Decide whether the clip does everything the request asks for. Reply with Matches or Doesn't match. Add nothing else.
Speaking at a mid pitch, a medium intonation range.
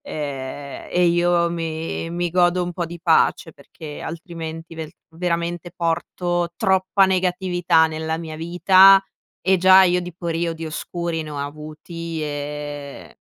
Doesn't match